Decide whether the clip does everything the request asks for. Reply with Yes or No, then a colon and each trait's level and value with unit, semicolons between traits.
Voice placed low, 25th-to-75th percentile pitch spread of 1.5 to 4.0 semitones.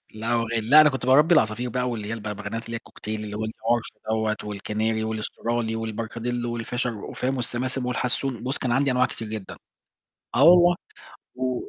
Yes: low, 115 Hz; narrow, 2.5 semitones